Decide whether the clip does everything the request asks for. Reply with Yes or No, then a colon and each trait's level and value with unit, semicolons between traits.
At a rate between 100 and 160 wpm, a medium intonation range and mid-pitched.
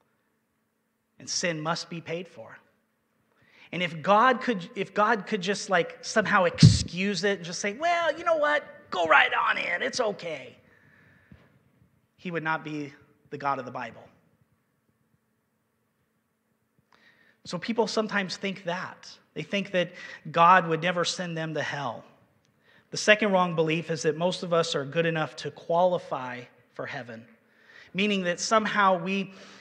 Yes: average, 150 wpm; average, 4.1 semitones; medium, 180 Hz